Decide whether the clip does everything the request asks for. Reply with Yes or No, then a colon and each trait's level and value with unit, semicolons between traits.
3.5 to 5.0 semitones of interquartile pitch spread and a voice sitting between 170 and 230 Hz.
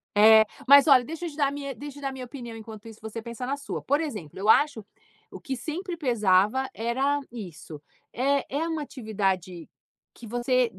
No: average, 4.5 semitones; very high, 250 Hz